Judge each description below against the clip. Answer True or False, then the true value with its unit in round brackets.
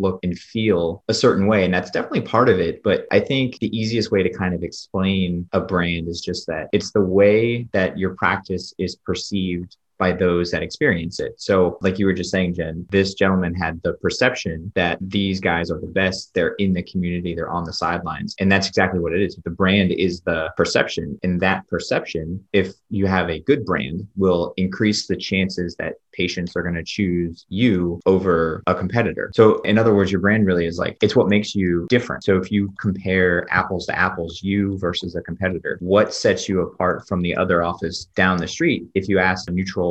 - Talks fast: True (210 wpm)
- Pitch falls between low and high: False (95 Hz)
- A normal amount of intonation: False (1.8 semitones)